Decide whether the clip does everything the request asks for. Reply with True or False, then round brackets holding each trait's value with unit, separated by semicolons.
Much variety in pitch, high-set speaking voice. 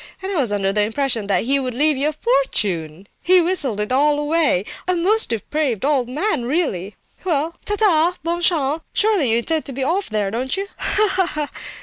True (6.4 semitones; 285 Hz)